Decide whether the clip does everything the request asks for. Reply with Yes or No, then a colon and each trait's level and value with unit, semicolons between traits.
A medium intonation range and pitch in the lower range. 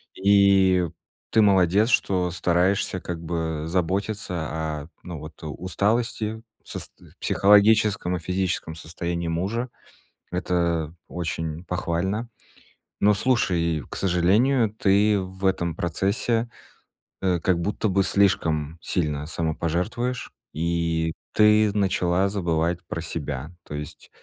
Yes: average, 3.3 semitones; very low, 90 Hz